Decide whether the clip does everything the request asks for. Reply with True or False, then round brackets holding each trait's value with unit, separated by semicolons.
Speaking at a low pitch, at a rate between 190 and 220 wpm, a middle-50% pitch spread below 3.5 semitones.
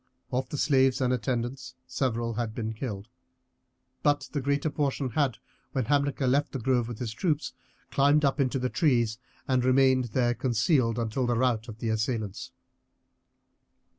False (125 Hz; 155 wpm; 2.8 semitones)